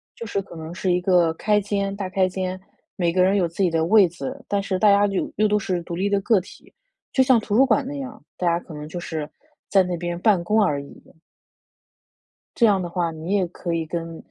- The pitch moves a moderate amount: Yes, average, 3.0 semitones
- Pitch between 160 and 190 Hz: Yes, medium, 185 Hz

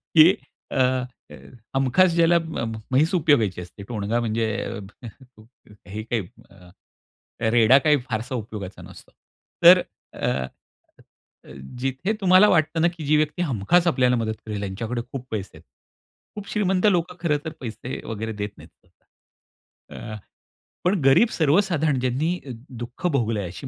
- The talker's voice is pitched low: Yes, low, 130 Hz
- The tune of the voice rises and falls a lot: Yes, wide, 7.0 semitones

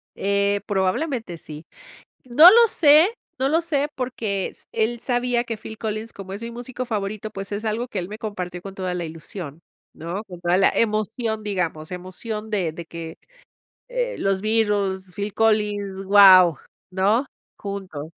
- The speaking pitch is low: No, high, 205 Hz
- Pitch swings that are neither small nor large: Yes, average, 3.7 semitones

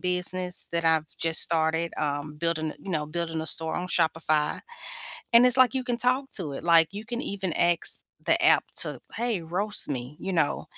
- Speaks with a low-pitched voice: No, medium, 170 Hz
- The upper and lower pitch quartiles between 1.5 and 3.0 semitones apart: No, average, 3.8 semitones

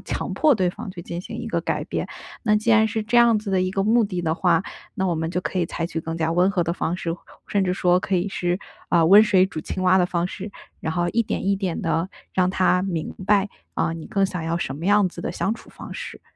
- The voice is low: No, medium, 185 Hz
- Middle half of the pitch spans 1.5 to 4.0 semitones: Yes, average, 2.8 semitones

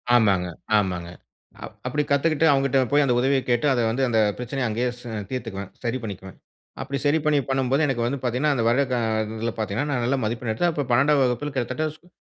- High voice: No, low, 130 Hz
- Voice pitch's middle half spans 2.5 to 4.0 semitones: Yes, average, 3.5 semitones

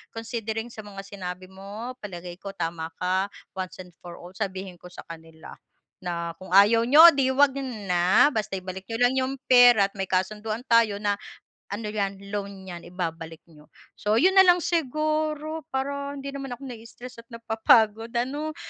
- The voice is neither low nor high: No, high, 215 Hz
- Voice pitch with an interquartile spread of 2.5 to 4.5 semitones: No, average, 5.3 semitones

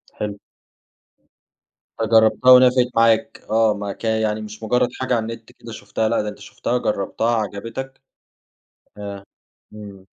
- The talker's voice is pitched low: Yes, low, 110 Hz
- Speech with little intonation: Yes, narrow, 1.8 semitones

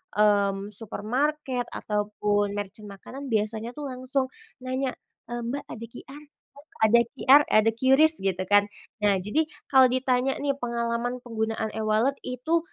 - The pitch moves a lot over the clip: No, average, 3.9 semitones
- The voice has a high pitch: Yes, high, 235 Hz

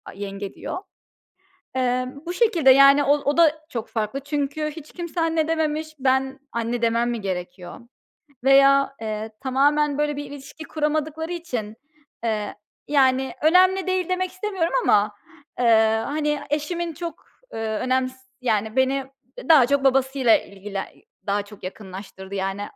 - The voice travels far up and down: Yes, wide, 5.8 semitones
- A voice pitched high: Yes, very high, 270 Hz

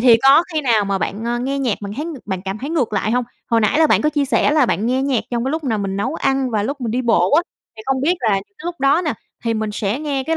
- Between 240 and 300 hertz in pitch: Yes, very high, 250 Hz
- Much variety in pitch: No, average, 4.7 semitones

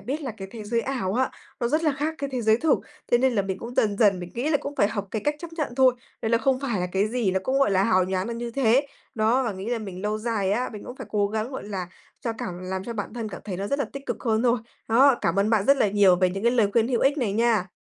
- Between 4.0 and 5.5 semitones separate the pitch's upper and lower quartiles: Yes, average, 4.4 semitones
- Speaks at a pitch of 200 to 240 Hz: Yes, high, 225 Hz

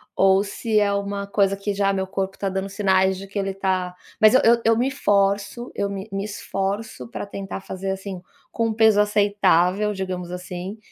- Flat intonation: Yes, narrow, 1.3 semitones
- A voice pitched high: Yes, high, 195 Hz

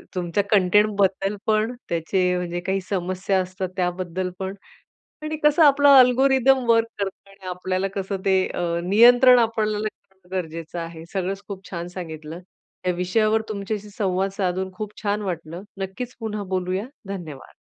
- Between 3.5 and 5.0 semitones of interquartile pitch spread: No, average, 3.0 semitones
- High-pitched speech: Yes, high, 195 Hz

